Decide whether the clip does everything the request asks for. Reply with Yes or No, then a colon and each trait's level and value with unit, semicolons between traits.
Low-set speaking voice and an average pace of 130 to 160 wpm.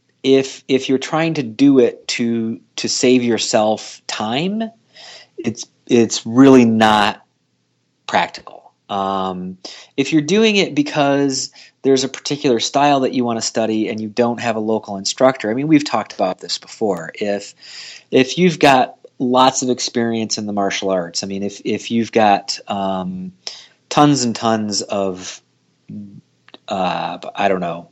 Yes: low, 115 Hz; average, 155 wpm